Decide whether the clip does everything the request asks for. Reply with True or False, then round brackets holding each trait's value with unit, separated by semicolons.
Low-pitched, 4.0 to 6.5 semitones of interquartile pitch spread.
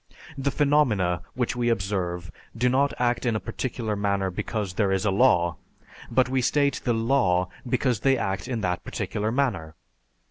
True (115 Hz; 5.1 semitones)